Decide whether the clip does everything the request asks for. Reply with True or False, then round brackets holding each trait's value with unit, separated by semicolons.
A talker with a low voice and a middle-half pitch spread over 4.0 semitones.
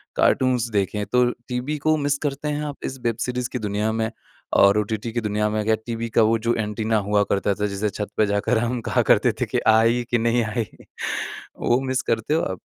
False (115 Hz; 2.9 semitones)